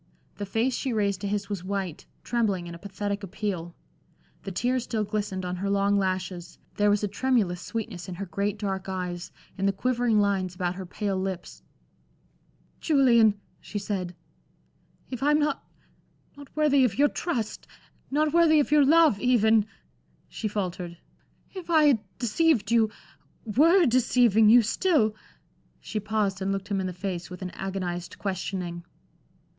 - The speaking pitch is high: Yes, high, 205 Hz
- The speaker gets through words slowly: No, average, 160 wpm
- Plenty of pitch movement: No, average, 4.4 semitones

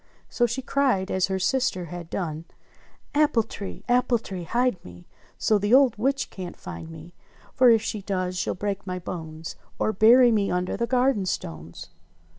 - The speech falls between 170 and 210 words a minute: Yes, average, 175 wpm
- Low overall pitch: No, high, 200 Hz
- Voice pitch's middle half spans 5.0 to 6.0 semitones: Yes, average, 5.3 semitones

